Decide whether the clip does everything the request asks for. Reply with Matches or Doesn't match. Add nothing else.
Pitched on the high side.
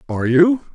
Doesn't match